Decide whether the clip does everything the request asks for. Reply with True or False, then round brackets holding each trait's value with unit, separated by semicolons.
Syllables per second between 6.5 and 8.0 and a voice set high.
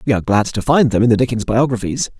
False (6.9 syllables/s; 120 Hz)